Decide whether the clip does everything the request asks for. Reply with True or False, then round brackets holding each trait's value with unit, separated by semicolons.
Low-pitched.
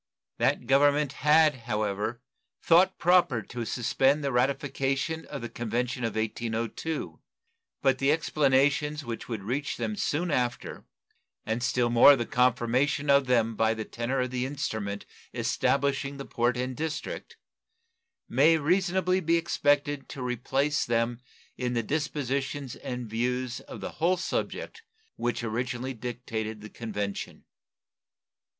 True (130 Hz)